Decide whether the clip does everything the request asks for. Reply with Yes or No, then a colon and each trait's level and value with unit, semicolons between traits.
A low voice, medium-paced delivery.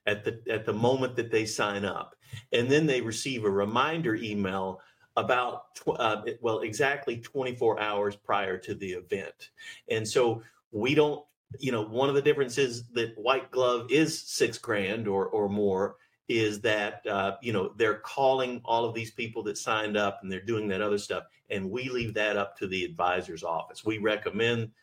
Yes: low, 115 Hz; average, 185 wpm